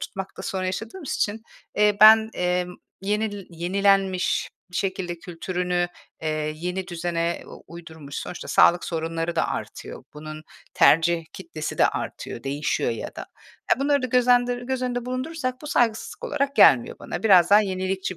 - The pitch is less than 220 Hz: Yes, high, 190 Hz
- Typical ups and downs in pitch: Yes, average, 4.5 semitones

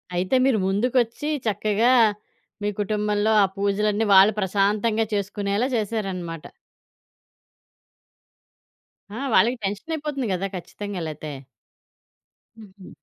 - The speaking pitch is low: No, high, 205 Hz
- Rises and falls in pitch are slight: Yes, narrow, 2.3 semitones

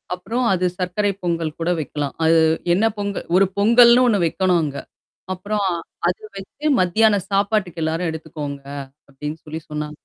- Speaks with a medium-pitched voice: Yes, medium, 180 Hz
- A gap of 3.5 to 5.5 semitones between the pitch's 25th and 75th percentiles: Yes, average, 4.2 semitones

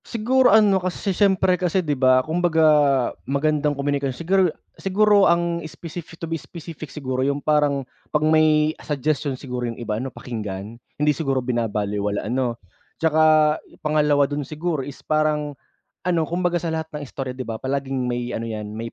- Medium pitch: Yes, medium, 150 Hz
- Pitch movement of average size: Yes, average, 4.2 semitones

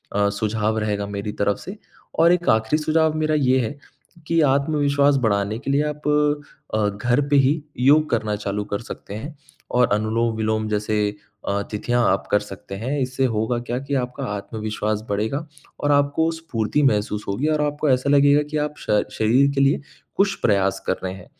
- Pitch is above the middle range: No, low, 120 Hz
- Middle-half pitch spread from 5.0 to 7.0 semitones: Yes, wide, 5.5 semitones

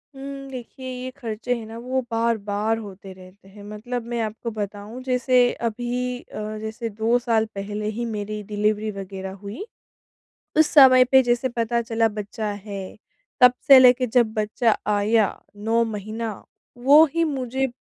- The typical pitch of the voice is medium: No, high, 225 Hz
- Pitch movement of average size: Yes, average, 3.0 semitones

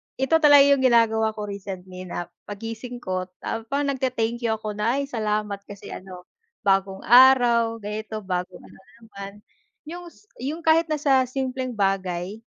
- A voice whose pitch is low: No, high, 225 Hz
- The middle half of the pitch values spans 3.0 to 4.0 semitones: No, average, 4.7 semitones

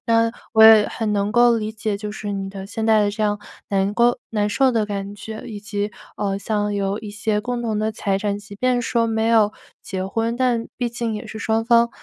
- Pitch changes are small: Yes, narrow, 1.9 semitones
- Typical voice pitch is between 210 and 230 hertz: Yes, high, 215 Hz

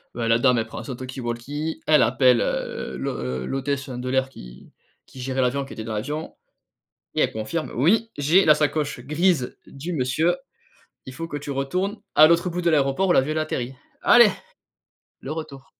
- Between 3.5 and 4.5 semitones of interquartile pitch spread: Yes, average, 3.8 semitones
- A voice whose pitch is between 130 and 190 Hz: Yes, low, 135 Hz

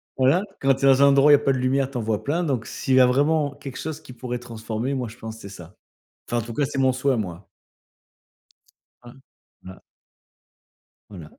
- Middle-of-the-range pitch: No, low, 130 Hz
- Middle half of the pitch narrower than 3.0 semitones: No, average, 3.5 semitones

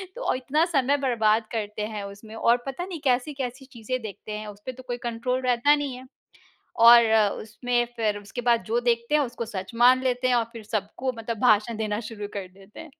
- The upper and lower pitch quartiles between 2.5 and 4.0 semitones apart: Yes, average, 3.1 semitones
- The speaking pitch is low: No, high, 235 Hz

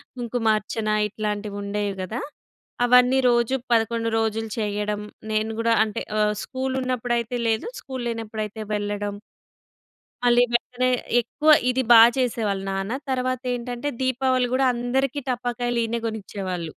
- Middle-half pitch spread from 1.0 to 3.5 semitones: Yes, average, 2.8 semitones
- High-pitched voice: Yes, high, 230 Hz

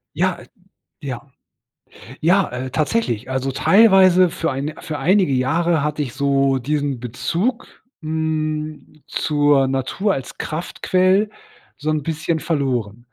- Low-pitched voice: No, medium, 150 Hz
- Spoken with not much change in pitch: No, average, 4.0 semitones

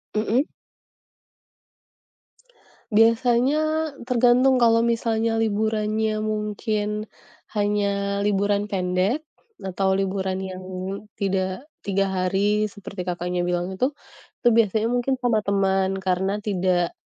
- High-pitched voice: Yes, high, 210 Hz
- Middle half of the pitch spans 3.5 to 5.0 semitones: No, average, 3.0 semitones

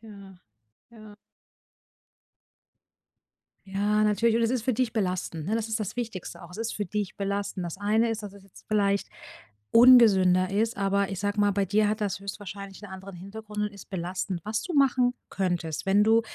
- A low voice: No, high, 205 Hz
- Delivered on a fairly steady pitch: Yes, narrow, 2.3 semitones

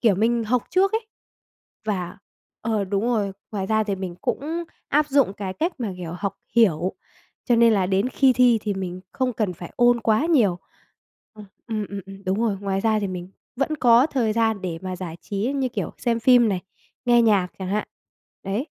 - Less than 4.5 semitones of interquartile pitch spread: Yes, average, 4.0 semitones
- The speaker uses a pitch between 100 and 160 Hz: No, high, 215 Hz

